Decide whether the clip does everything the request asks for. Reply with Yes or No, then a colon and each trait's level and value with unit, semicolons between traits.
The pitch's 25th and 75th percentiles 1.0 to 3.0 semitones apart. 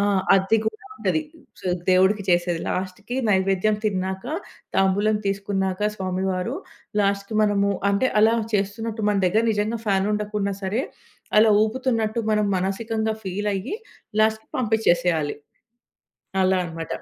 Yes: narrow, 2.4 semitones